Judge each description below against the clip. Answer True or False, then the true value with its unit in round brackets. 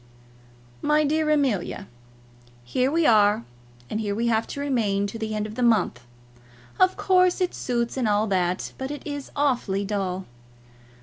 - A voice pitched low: False (230 Hz)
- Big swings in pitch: True (6.0 semitones)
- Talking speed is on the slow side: False (165 wpm)